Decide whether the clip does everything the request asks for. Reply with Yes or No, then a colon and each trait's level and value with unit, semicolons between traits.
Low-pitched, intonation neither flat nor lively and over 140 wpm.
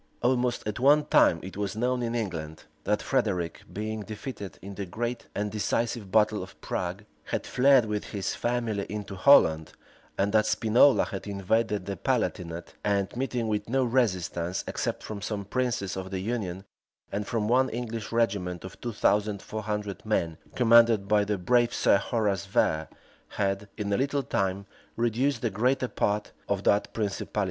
Yes: low, 105 Hz; average, 3.2 semitones; average, 170 wpm